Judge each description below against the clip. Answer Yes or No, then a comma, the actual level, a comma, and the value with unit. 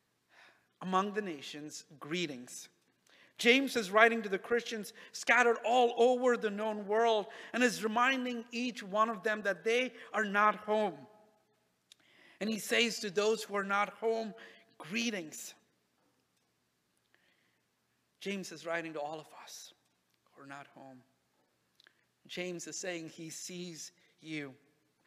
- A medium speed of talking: No, slow, 130 wpm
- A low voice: No, high, 205 Hz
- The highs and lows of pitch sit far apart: Yes, wide, 6.5 semitones